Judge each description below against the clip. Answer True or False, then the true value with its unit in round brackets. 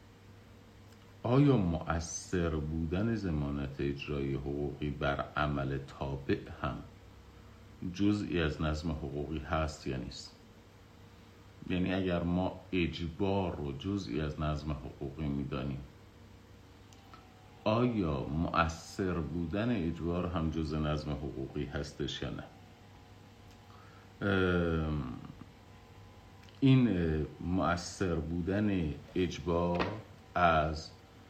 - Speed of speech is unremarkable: False (80 wpm)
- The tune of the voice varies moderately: True (4.3 semitones)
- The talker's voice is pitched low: True (90 Hz)